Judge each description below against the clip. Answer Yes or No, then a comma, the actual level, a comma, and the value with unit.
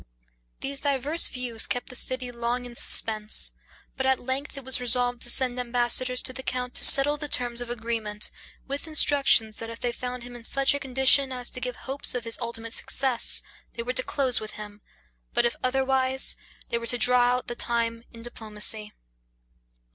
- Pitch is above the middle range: Yes, high, 245 Hz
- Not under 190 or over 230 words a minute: Yes, average, 195 wpm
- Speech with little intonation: Yes, narrow, 2.0 semitones